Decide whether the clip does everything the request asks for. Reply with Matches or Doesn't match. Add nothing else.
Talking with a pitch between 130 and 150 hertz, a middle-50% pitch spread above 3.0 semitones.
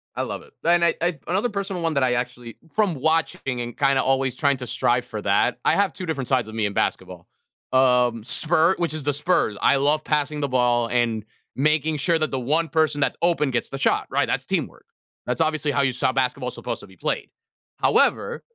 Matches